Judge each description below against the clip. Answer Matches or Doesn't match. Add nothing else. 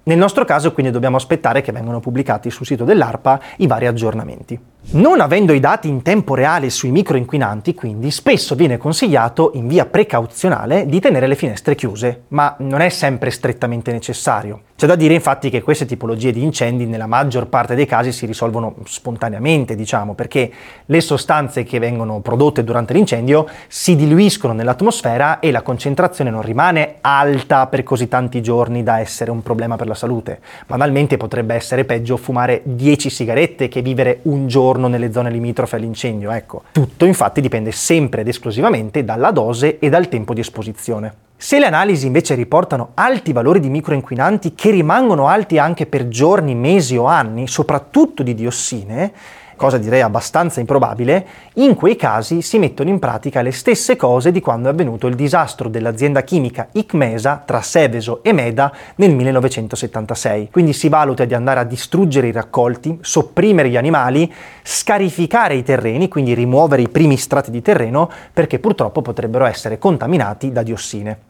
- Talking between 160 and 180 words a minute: Matches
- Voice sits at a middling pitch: Doesn't match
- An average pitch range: Matches